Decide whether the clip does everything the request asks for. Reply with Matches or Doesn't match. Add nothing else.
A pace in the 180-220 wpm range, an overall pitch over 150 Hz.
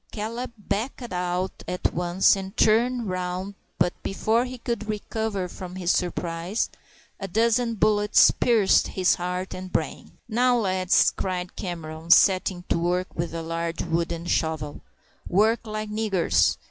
Doesn't match